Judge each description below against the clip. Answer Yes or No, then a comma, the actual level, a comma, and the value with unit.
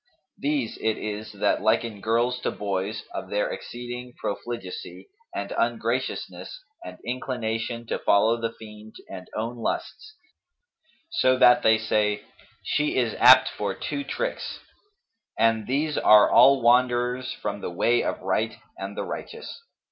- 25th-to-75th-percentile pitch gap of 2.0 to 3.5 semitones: Yes, average, 3.0 semitones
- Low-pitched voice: Yes, low, 115 Hz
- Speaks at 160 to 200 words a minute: No, average, 140 wpm